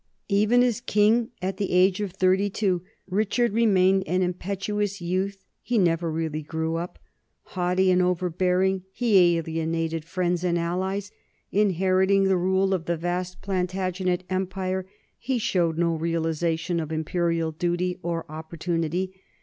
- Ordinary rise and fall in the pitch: No, narrow, 2.3 semitones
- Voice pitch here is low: No, medium, 180 Hz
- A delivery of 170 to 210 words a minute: No, average, 140 wpm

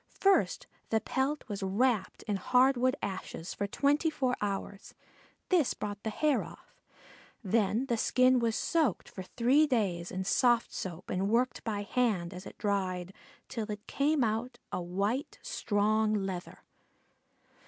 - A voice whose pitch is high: Yes, high, 220 Hz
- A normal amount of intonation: Yes, average, 4.6 semitones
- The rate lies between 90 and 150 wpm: Yes, average, 145 wpm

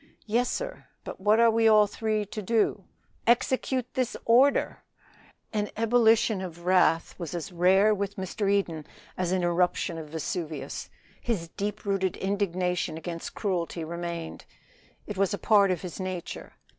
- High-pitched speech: Yes, high, 195 Hz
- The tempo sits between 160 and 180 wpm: No, average, 150 wpm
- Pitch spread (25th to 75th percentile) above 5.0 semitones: No, average, 3.7 semitones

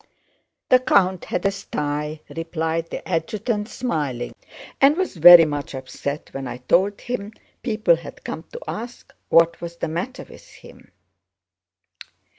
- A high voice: No, medium, 170 Hz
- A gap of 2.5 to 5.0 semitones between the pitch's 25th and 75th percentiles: No, wide, 5.4 semitones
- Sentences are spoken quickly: No, average, 140 wpm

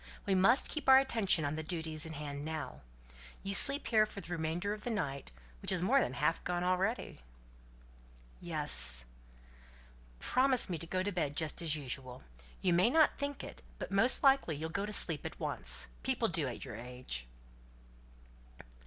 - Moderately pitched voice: Yes, medium, 175 Hz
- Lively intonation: Yes, wide, 6.3 semitones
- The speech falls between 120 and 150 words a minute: No, average, 180 wpm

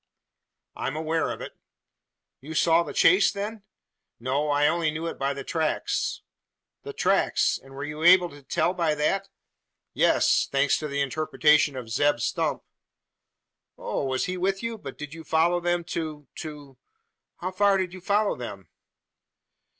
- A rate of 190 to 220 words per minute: No, average, 165 wpm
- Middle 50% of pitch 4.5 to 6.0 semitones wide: No, average, 3.6 semitones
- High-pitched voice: No, medium, 155 Hz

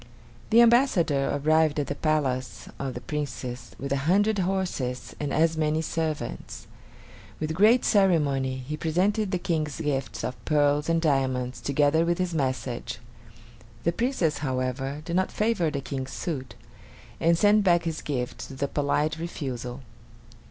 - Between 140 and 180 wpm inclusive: Yes, average, 150 wpm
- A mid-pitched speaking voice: Yes, medium, 150 Hz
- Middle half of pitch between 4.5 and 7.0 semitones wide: No, average, 4.1 semitones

